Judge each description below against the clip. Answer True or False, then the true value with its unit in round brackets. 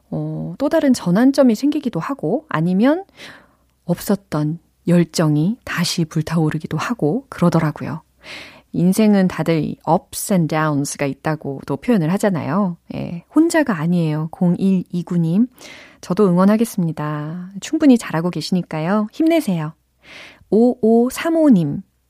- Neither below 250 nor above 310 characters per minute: True (275 characters per minute)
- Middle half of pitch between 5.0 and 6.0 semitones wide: False (6.6 semitones)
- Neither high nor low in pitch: True (180 Hz)